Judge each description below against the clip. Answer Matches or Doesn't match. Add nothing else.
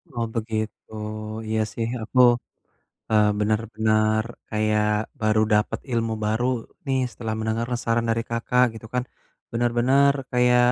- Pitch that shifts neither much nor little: Doesn't match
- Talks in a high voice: Doesn't match